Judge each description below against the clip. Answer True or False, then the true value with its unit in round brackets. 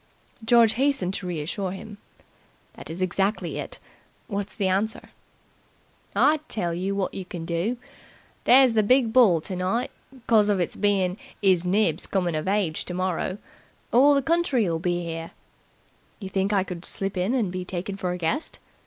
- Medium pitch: False (195 Hz)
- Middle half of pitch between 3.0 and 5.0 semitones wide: True (3.5 semitones)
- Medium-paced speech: True (160 wpm)